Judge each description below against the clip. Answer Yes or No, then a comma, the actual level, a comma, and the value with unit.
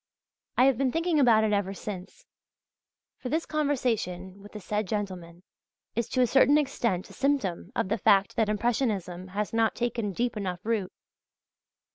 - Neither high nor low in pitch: No, high, 215 Hz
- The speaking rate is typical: Yes, average, 165 wpm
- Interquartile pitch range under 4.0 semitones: No, average, 4.6 semitones